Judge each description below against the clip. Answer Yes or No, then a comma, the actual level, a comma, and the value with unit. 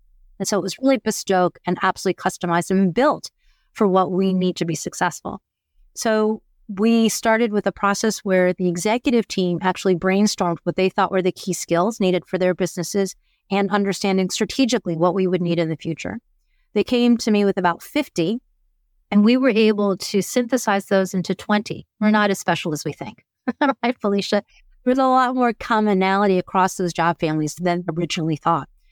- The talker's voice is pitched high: Yes, high, 195 Hz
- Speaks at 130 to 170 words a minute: No, average, 185 wpm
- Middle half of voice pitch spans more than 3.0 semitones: Yes, average, 3.4 semitones